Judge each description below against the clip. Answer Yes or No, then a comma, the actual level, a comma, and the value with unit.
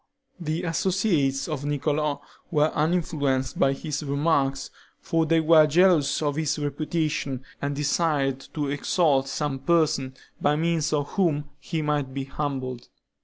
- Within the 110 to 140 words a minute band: Yes, slow, 135 wpm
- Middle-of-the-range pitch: Yes, medium, 150 Hz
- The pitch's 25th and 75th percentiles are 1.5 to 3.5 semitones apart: Yes, narrow, 2.6 semitones